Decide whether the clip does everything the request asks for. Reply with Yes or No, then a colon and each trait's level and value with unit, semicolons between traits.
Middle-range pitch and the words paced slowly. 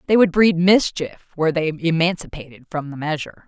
No: medium, 165 Hz; average, 170 wpm